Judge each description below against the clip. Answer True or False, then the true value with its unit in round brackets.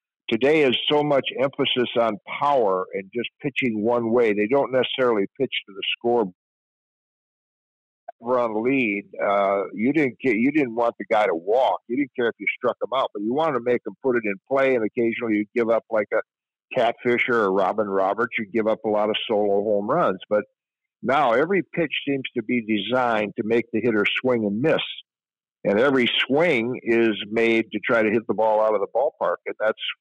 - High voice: False (115 Hz)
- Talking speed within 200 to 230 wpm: True (205 wpm)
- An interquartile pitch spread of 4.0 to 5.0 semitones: False (2.7 semitones)